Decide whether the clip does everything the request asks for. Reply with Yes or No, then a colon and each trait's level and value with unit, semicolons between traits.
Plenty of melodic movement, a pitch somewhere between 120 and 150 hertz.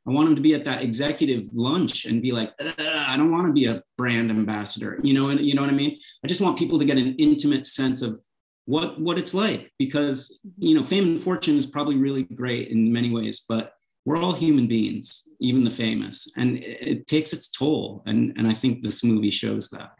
Yes: wide, 5.9 semitones; low, 135 Hz